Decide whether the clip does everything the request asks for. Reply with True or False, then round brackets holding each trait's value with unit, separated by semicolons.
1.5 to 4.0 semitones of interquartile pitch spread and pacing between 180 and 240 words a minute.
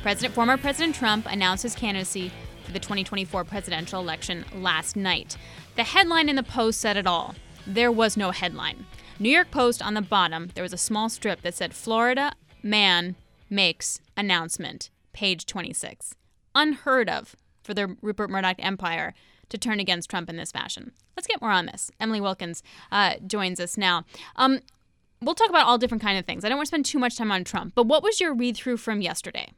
False (4.8 semitones; 195 wpm)